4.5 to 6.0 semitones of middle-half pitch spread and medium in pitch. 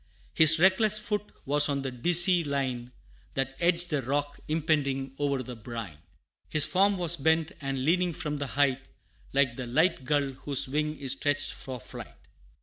No: average, 3.5 semitones; medium, 145 Hz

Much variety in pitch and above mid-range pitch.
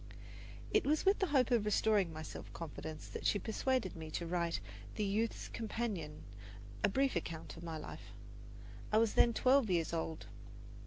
Yes: wide, 6.1 semitones; high, 200 Hz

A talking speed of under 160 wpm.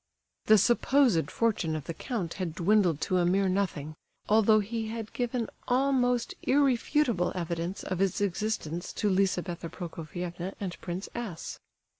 Yes: average, 140 wpm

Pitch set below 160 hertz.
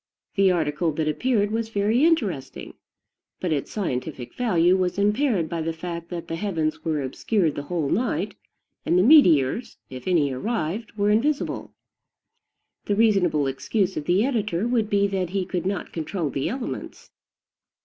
No: medium, 185 Hz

